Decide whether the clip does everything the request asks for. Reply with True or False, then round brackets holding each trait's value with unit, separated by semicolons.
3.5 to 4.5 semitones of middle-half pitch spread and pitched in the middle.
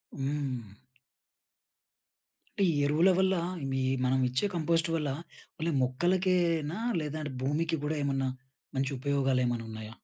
True (4.0 semitones; 145 Hz)